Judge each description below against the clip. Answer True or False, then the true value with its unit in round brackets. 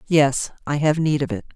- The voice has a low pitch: False (145 Hz)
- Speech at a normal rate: False (230 wpm)